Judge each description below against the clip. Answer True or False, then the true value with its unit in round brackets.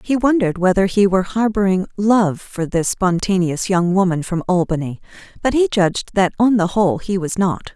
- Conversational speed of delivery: True (185 wpm)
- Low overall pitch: False (190 Hz)